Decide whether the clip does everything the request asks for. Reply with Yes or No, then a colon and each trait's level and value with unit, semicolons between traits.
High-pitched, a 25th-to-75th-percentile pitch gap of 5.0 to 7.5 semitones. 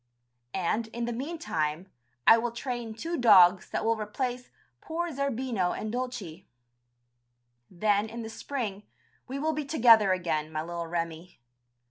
Yes: high, 225 Hz; wide, 5.6 semitones